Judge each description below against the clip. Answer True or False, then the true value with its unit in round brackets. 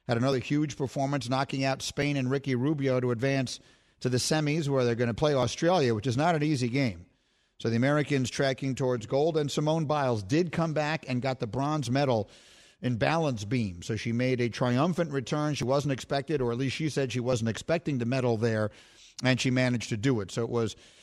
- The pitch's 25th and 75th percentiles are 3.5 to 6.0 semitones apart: False (2.9 semitones)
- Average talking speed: False (215 wpm)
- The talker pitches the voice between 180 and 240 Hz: False (130 Hz)